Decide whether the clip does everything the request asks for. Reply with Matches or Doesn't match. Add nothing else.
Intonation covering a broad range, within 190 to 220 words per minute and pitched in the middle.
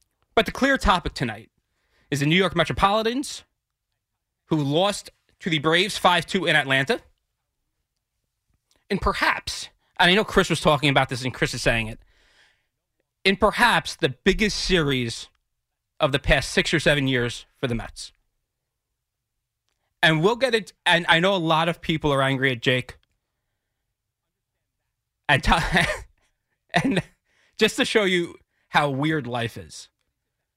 Doesn't match